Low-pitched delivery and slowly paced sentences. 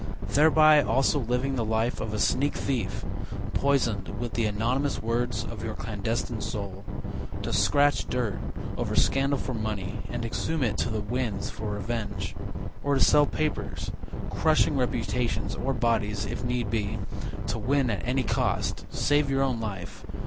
No: low, 120 Hz; average, 155 wpm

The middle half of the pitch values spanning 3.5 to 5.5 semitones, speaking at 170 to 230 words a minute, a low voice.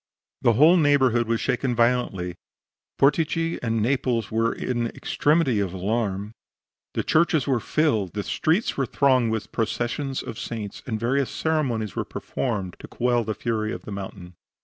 No: average, 4.0 semitones; average, 160 wpm; low, 120 Hz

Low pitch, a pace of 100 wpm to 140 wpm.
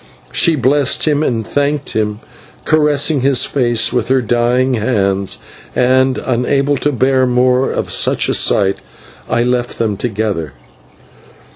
Yes: low, 125 Hz; slow, 135 wpm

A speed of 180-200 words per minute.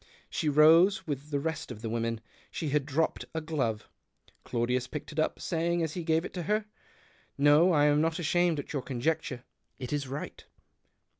Yes: average, 195 wpm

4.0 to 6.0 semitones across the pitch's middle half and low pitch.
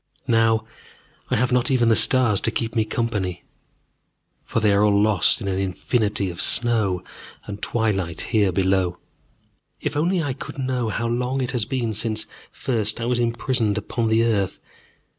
No: average, 3.1 semitones; low, 110 Hz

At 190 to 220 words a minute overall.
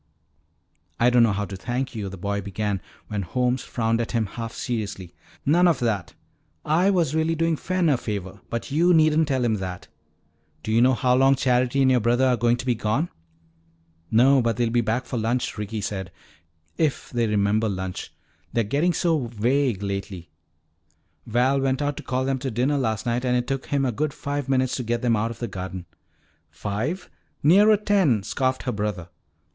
Yes: average, 195 wpm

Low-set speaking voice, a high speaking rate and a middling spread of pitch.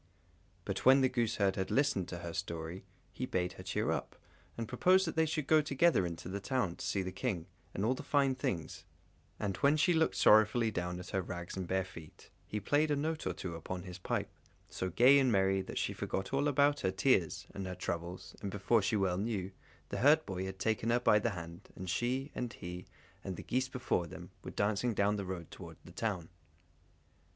No: low, 100 Hz; fast, 215 wpm; wide, 6.1 semitones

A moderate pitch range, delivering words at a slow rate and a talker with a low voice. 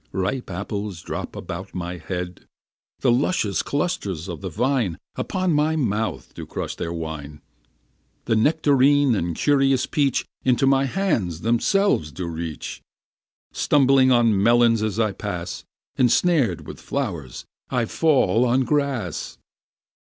No: wide, 7.2 semitones; slow, 130 wpm; low, 115 Hz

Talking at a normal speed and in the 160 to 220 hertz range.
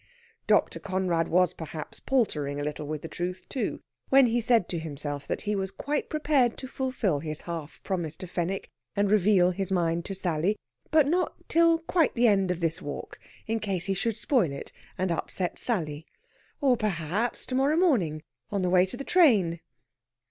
Yes: average, 185 wpm; high, 190 Hz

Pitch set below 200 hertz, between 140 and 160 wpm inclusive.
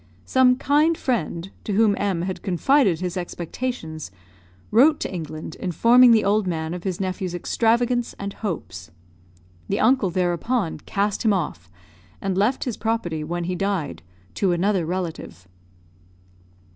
Yes: high, 190 Hz; average, 145 wpm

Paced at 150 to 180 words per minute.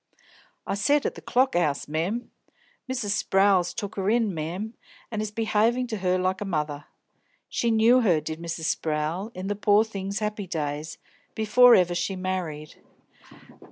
Yes: average, 160 wpm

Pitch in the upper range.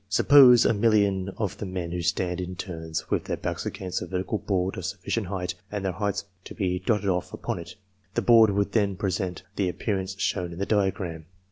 No: very low, 95 Hz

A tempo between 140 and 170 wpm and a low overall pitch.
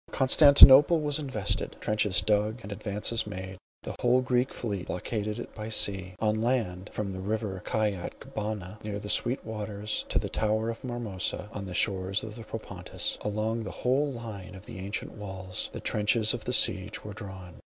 No: average, 180 wpm; low, 105 Hz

